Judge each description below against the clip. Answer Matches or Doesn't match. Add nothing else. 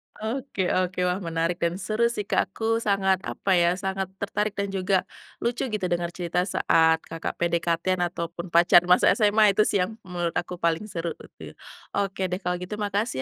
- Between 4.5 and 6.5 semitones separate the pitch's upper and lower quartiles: Doesn't match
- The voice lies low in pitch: Doesn't match